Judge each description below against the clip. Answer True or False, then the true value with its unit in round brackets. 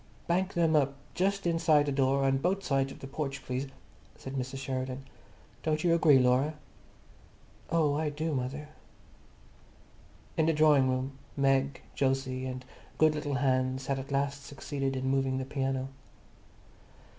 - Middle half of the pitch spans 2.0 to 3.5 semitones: True (2.4 semitones)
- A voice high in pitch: False (135 Hz)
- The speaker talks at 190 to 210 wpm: False (150 wpm)